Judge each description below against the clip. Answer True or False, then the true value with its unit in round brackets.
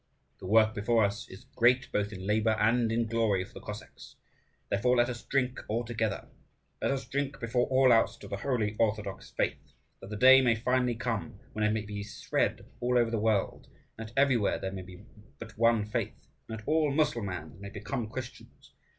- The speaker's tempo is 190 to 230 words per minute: True (200 wpm)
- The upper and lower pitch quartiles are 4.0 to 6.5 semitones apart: False (2.9 semitones)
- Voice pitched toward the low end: True (115 Hz)